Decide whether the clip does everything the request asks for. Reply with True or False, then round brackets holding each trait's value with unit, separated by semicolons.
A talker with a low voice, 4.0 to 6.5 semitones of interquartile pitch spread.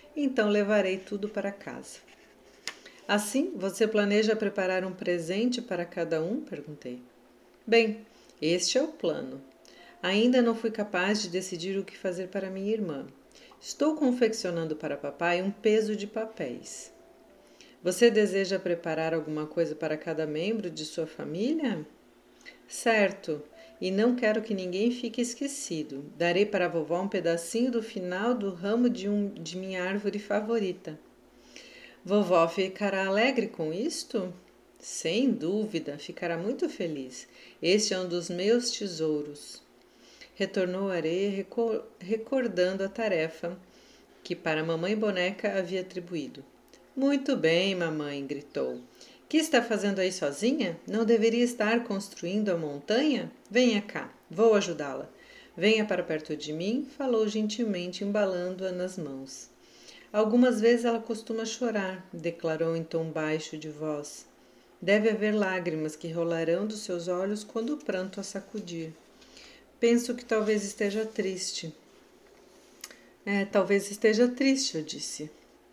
False (195 Hz; 4.8 semitones)